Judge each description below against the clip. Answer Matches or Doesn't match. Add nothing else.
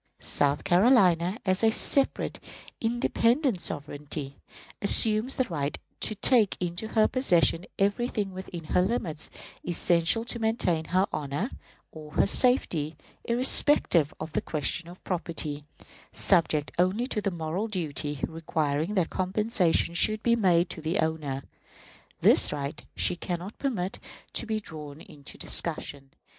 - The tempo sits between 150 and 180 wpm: Doesn't match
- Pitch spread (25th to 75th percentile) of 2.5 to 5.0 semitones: Doesn't match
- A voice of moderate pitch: Matches